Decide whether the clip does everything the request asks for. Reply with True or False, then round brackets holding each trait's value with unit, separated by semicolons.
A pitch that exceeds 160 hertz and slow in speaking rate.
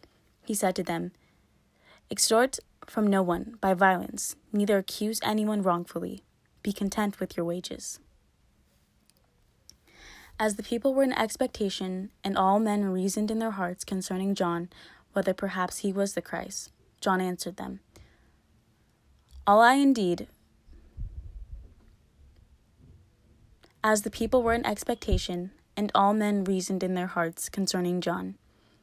True (190 Hz; 125 wpm)